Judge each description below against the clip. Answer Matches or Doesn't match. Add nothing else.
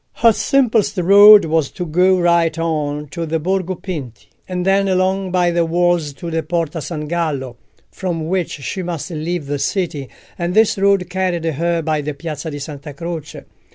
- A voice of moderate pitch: Matches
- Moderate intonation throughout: Matches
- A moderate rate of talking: Matches